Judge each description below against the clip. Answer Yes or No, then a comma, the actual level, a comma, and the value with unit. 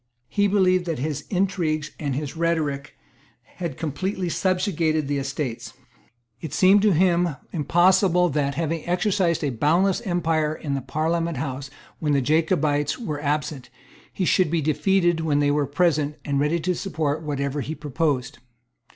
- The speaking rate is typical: Yes, average, 150 wpm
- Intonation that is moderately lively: Yes, average, 3.4 semitones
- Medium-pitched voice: Yes, medium, 155 Hz